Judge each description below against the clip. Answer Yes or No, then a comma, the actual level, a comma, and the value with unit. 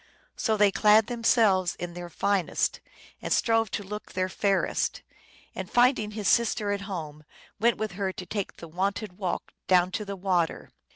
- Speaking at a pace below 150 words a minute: No, average, 170 wpm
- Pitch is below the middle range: No, high, 200 Hz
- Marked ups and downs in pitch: No, average, 2.8 semitones